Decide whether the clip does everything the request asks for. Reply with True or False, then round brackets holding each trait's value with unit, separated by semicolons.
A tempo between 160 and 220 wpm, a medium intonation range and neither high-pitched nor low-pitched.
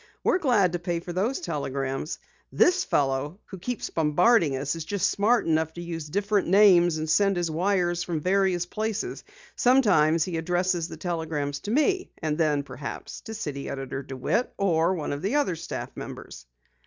True (175 wpm; 4.5 semitones; 175 Hz)